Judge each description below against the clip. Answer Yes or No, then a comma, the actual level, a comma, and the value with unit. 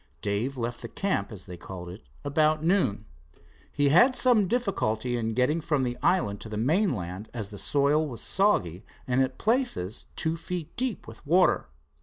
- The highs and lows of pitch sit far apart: Yes, wide, 8.5 semitones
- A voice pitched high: No, low, 135 Hz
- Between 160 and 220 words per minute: Yes, average, 175 wpm